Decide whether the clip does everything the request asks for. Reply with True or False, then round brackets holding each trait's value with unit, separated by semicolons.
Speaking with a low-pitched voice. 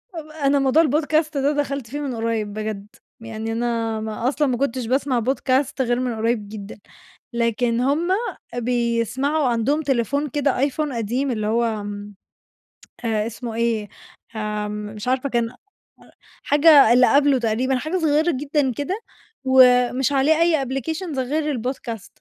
False (255 Hz)